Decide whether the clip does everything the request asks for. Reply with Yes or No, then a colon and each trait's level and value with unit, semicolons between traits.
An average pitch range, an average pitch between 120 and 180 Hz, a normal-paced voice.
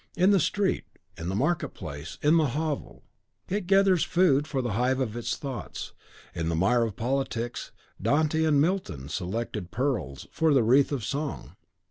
No: wide, 6.2 semitones; low, 135 Hz; average, 170 wpm